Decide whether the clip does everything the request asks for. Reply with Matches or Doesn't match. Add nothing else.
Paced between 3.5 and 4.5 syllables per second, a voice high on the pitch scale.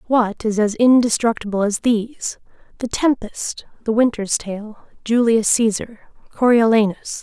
Matches